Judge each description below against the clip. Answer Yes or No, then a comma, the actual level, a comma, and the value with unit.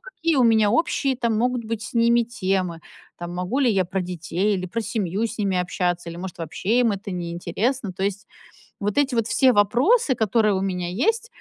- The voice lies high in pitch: Yes, high, 210 Hz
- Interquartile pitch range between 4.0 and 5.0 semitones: Yes, average, 4.6 semitones